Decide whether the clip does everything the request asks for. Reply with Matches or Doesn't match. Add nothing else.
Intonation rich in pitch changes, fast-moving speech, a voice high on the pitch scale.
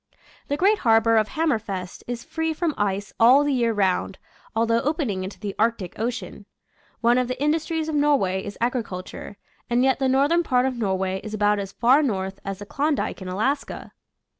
Doesn't match